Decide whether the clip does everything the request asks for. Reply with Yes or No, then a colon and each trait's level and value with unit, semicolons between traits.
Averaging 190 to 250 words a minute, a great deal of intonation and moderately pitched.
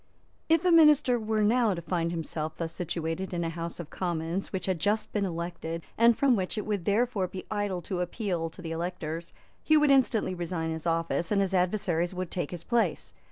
No: fast, 205 wpm; average, 4.2 semitones; medium, 180 Hz